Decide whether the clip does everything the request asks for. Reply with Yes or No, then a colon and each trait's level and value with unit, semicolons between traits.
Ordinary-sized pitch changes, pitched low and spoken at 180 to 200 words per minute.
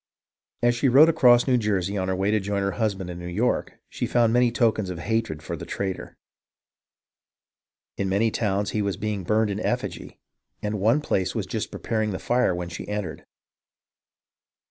Yes: average, 3.2 semitones; low, 105 Hz; average, 185 wpm